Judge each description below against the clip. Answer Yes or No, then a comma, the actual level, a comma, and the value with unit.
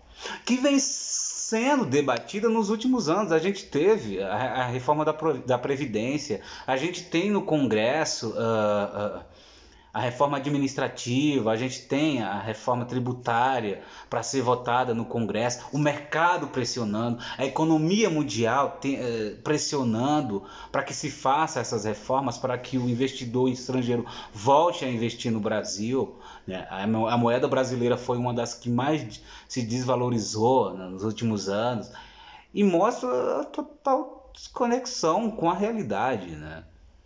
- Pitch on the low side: Yes, low, 130 Hz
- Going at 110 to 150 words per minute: Yes, average, 140 wpm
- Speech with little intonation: No, average, 5.0 semitones